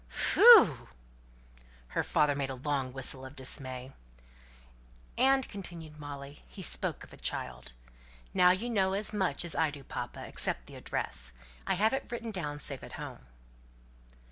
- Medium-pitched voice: Yes, medium, 150 Hz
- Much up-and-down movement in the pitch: Yes, wide, 6.7 semitones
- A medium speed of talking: Yes, average, 155 wpm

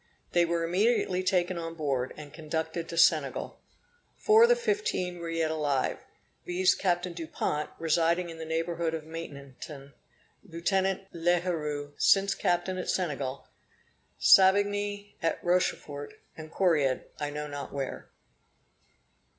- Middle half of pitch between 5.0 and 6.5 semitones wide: No, average, 3.4 semitones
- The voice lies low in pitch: No, medium, 165 Hz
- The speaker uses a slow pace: Yes, slow, 125 wpm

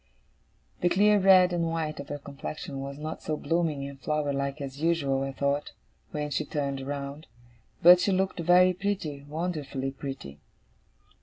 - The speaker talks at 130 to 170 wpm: Yes, average, 160 wpm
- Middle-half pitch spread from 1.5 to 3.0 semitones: No, average, 3.8 semitones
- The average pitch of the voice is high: No, medium, 150 Hz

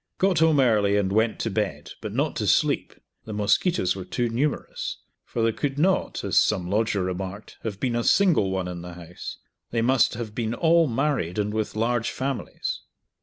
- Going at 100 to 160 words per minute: No, average, 190 wpm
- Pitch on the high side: No, low, 115 Hz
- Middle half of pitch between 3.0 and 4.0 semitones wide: No, average, 5.0 semitones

